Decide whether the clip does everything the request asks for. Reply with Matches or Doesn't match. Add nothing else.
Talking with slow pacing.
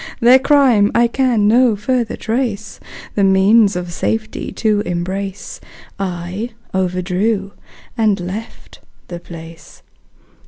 Matches